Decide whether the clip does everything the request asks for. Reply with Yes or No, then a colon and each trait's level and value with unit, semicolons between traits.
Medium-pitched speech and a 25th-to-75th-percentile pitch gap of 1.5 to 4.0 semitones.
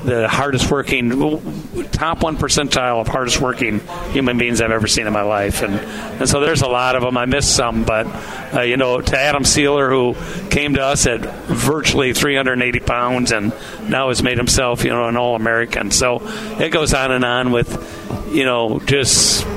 No: low, 125 Hz; average, 2.7 semitones